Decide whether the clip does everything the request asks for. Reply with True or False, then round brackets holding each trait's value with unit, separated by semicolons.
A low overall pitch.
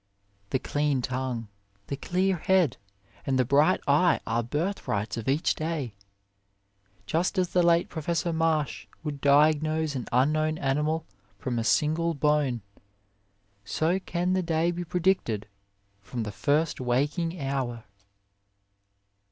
False (150 Hz)